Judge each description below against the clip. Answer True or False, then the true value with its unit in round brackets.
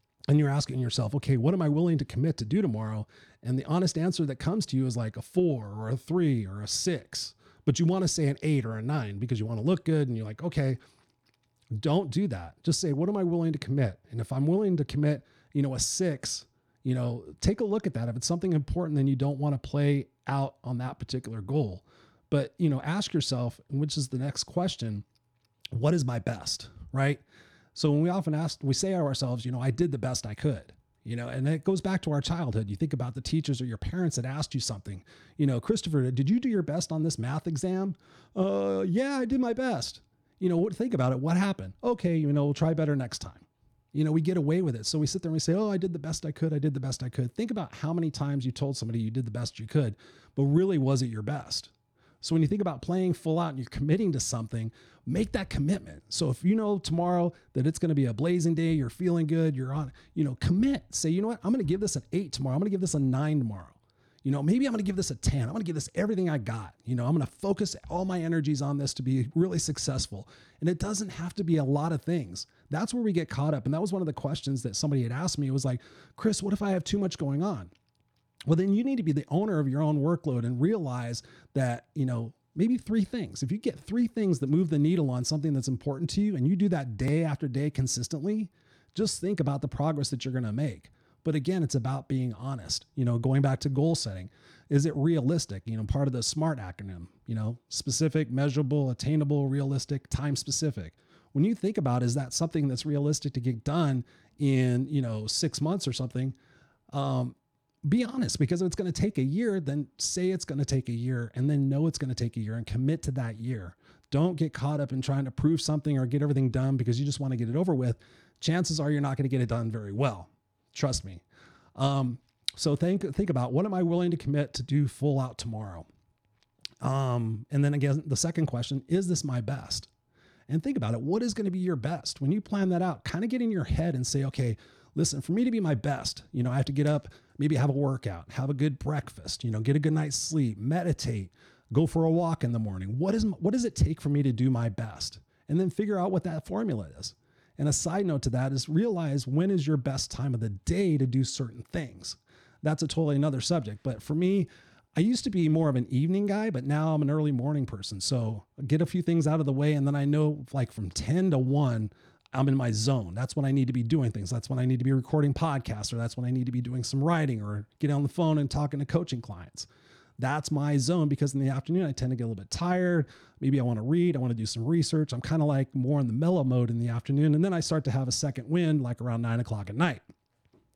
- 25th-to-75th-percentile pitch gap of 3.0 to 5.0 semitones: True (4.7 semitones)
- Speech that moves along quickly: True (265 wpm)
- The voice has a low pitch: False (145 Hz)